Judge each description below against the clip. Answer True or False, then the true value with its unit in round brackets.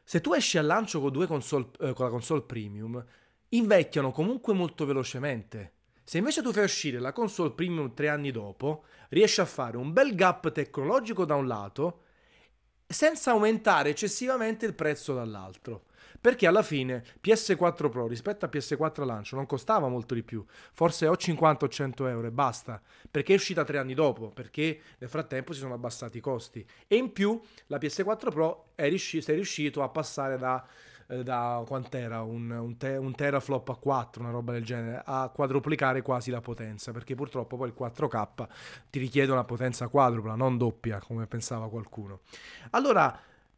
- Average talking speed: False (175 wpm)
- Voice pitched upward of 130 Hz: True (140 Hz)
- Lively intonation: False (4.8 semitones)